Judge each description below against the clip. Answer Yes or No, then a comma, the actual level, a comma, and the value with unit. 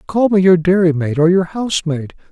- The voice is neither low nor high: Yes, medium, 175 Hz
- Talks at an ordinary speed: Yes, average, 180 wpm